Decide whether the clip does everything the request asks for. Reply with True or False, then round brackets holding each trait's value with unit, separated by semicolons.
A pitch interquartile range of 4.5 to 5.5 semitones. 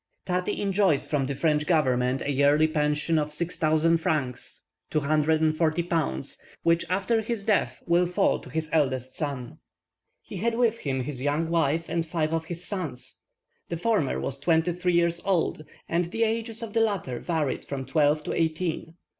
False (3.2 semitones)